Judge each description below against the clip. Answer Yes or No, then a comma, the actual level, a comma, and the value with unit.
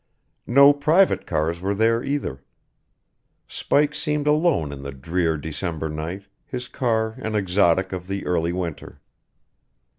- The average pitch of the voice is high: No, very low, 95 Hz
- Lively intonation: Yes, wide, 7.8 semitones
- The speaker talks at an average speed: No, slow, 130 wpm